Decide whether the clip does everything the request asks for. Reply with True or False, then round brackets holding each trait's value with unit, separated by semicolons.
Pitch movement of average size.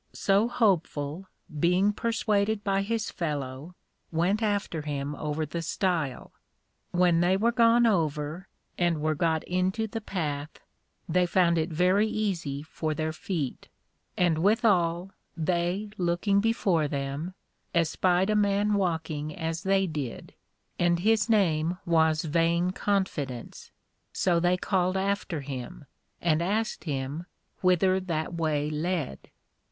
True (3.9 semitones)